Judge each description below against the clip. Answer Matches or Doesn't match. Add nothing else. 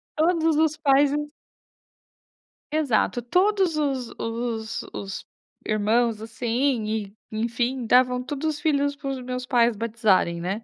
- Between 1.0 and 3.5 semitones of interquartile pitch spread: Doesn't match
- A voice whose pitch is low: Doesn't match